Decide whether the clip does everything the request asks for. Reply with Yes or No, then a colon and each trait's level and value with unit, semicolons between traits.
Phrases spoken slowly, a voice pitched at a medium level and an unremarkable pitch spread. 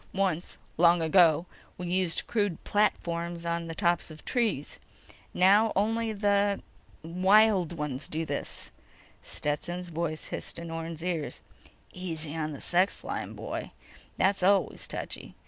Yes: slow, 130 wpm; medium, 175 Hz; average, 3.2 semitones